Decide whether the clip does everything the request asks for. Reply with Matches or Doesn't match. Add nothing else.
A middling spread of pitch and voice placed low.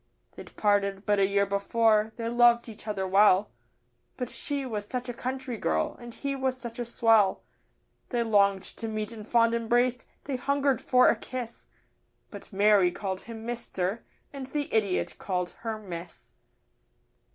Doesn't match